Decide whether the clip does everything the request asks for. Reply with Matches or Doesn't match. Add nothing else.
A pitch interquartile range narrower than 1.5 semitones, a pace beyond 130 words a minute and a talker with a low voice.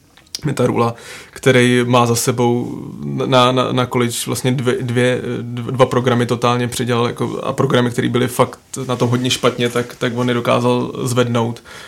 Matches